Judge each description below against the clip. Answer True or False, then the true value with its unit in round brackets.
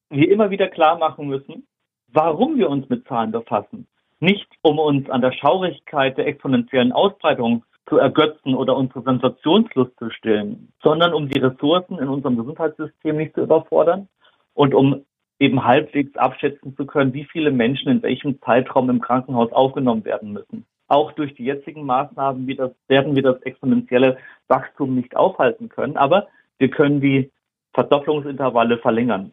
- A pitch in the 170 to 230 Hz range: False (135 Hz)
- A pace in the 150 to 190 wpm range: True (160 wpm)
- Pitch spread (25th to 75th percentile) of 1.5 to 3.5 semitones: True (3.2 semitones)